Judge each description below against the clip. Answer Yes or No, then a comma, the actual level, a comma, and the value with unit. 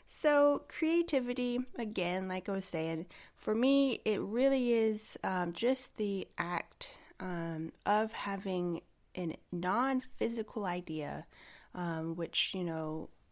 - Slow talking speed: Yes, slow, 120 wpm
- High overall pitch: Yes, high, 205 Hz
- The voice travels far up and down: Yes, wide, 6.0 semitones